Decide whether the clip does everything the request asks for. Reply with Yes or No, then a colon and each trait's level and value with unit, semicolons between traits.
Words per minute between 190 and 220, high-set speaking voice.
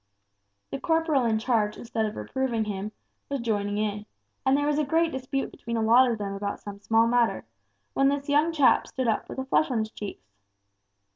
Yes: fast, 205 wpm; high, 235 Hz